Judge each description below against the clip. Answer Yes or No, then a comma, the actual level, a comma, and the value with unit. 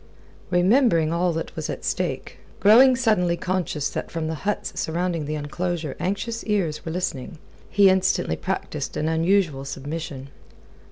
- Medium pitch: Yes, medium, 170 Hz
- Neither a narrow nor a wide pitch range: Yes, average, 3.9 semitones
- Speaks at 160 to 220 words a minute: No, average, 145 wpm